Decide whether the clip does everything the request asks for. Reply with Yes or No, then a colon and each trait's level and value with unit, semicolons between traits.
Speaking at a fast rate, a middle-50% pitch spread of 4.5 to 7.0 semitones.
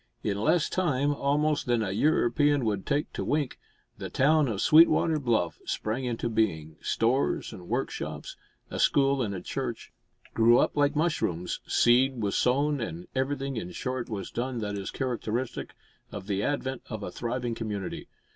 No: average, 165 wpm; average, 4.8 semitones